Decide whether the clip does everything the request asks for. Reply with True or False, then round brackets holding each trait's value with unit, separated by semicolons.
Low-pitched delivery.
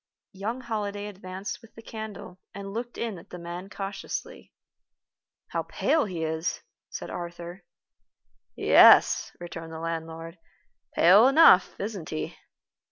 False (190 Hz)